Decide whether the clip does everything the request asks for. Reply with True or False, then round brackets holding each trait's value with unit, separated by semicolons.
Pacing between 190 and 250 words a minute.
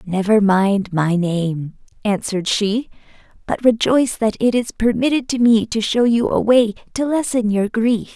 False (170 wpm)